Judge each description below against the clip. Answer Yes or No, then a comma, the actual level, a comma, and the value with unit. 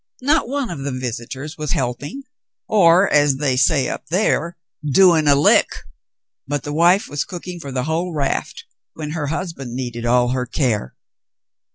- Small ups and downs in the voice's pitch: No, average, 4.8 semitones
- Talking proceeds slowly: No, average, 165 wpm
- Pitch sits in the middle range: Yes, medium, 145 Hz